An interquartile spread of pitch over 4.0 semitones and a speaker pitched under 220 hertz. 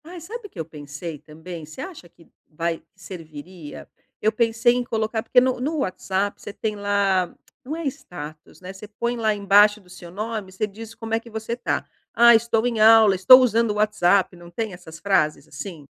Yes: average, 4.5 semitones; high, 205 Hz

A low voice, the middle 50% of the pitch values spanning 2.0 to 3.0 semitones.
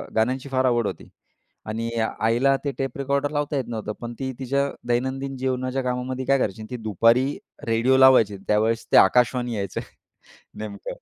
Yes: low, 125 Hz; average, 2.7 semitones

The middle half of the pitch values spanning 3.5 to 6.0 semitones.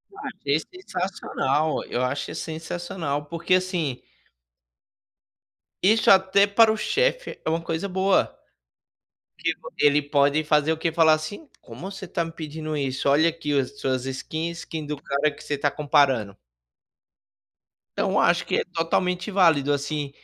Yes: average, 4.0 semitones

